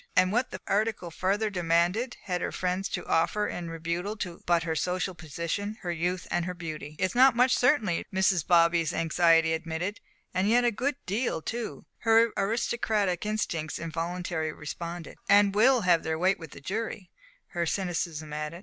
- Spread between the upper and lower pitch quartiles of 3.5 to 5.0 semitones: Yes, average, 3.9 semitones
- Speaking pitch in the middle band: Yes, medium, 180 Hz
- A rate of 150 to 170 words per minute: Yes, average, 165 wpm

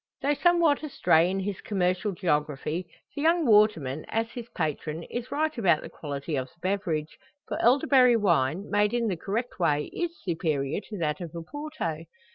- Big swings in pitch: Yes, wide, 7.2 semitones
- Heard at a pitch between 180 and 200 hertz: Yes, high, 190 Hz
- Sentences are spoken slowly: No, average, 170 wpm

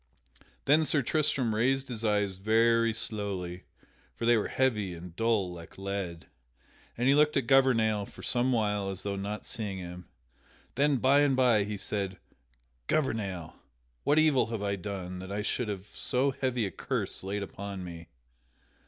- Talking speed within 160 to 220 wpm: Yes, average, 165 wpm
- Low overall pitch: Yes, low, 105 Hz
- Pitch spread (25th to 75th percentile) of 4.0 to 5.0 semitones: Yes, average, 4.5 semitones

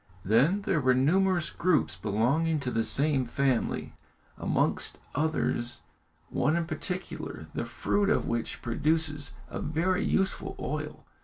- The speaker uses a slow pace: Yes, slow, 130 wpm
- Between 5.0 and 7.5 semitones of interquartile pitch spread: Yes, wide, 5.5 semitones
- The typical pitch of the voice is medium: Yes, medium, 150 Hz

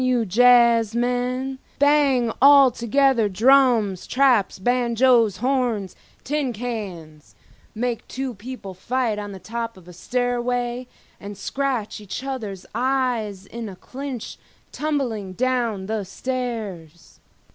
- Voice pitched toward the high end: Yes, high, 240 Hz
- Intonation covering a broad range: No, average, 3.7 semitones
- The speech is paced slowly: Yes, slow, 105 wpm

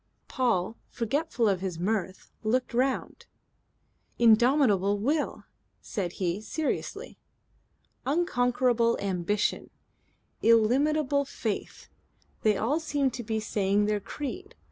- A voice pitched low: No, high, 230 Hz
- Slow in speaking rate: Yes, slow, 100 wpm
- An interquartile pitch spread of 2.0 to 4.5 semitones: No, average, 5.0 semitones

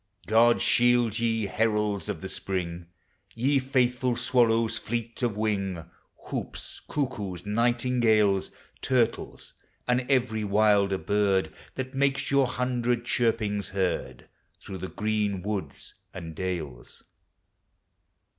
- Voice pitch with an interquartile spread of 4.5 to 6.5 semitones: No, average, 3.6 semitones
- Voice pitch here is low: Yes, low, 110 Hz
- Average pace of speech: No, slow, 110 wpm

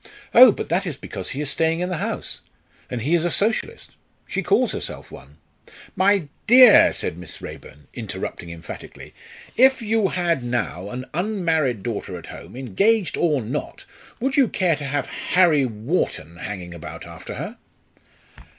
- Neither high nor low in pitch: Yes, medium, 150 Hz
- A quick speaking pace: No, average, 165 wpm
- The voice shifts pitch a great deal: Yes, wide, 9.0 semitones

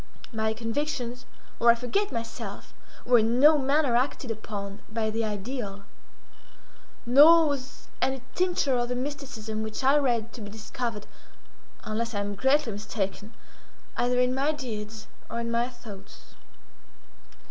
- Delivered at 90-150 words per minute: Yes, average, 140 wpm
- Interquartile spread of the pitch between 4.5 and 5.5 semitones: No, average, 3.5 semitones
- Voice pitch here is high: Yes, high, 235 Hz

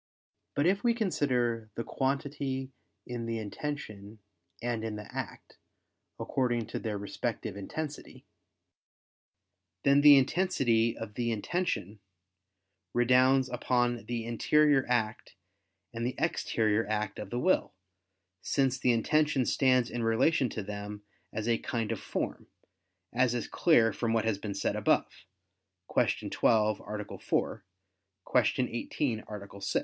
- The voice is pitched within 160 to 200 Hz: No, low, 120 Hz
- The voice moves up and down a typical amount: Yes, average, 3.5 semitones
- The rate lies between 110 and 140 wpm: Yes, slow, 135 wpm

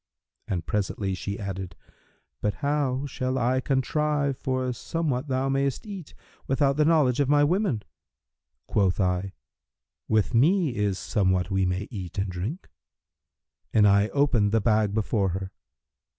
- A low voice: Yes, low, 115 Hz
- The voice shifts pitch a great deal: Yes, wide, 6.1 semitones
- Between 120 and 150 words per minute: Yes, average, 140 wpm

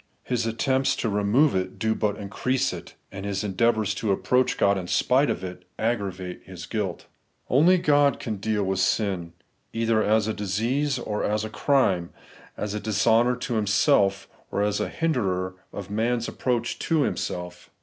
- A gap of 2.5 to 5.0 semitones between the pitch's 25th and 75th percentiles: Yes, average, 3.9 semitones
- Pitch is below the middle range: Yes, low, 110 Hz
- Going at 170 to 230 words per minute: Yes, average, 175 wpm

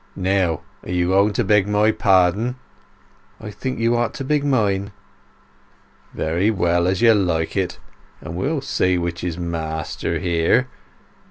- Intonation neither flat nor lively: Yes, average, 3.7 semitones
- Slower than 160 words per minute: Yes, average, 140 wpm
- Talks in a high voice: No, very low, 95 Hz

